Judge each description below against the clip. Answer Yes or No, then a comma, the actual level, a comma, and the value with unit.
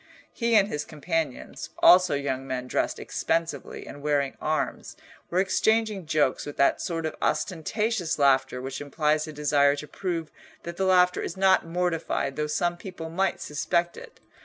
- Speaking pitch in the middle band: Yes, medium, 160 Hz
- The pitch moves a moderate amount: Yes, average, 3.8 semitones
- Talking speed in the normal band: Yes, average, 160 wpm